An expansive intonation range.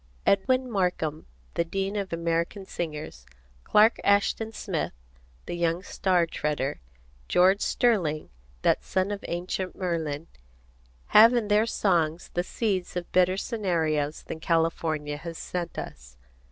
No: average, 3.6 semitones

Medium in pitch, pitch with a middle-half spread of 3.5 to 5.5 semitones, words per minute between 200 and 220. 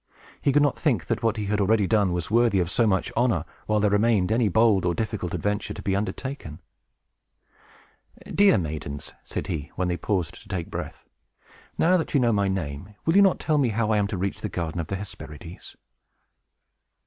No: low, 105 Hz; average, 4.4 semitones; fast, 205 wpm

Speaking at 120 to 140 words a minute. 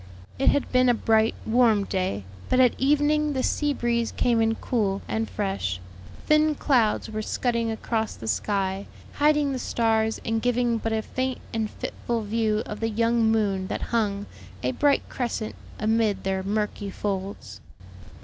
No: average, 160 wpm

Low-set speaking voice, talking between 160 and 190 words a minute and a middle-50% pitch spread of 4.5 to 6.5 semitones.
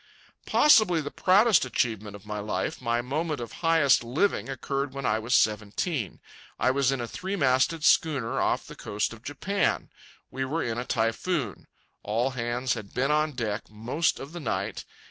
Yes: low, 130 Hz; average, 175 wpm; average, 5.3 semitones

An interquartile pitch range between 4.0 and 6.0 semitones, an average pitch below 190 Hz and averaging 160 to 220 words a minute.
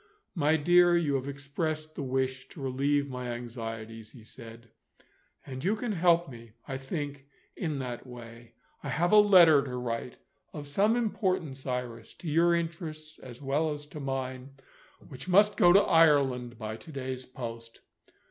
Yes: average, 4.5 semitones; medium, 140 Hz; average, 165 wpm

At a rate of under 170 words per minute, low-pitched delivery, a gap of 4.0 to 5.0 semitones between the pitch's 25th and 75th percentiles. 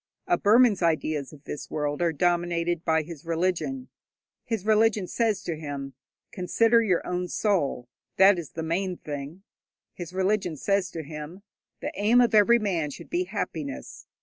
No: average, 160 wpm; medium, 175 Hz; average, 4.5 semitones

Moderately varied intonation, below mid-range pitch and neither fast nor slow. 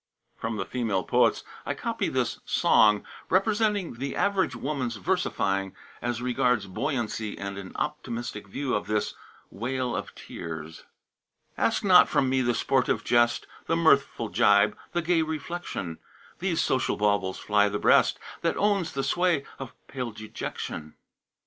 No: wide, 7.2 semitones; low, 120 Hz; average, 145 wpm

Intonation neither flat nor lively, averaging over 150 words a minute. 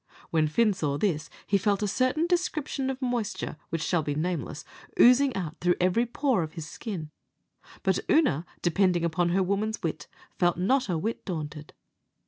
No: wide, 6.6 semitones; average, 170 wpm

